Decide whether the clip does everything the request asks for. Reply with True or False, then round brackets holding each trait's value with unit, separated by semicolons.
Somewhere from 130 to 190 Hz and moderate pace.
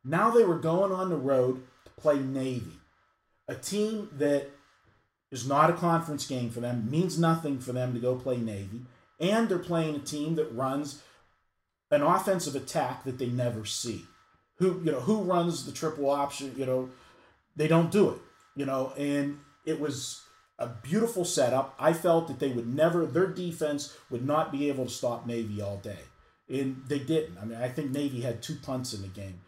True (140 Hz; 195 wpm)